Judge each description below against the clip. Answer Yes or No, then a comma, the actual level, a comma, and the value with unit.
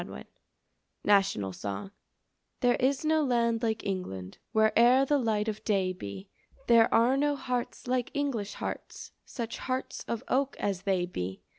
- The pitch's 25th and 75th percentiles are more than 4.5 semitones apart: Yes, average, 4.9 semitones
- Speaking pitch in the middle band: No, high, 225 Hz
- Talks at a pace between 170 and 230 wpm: No, average, 150 wpm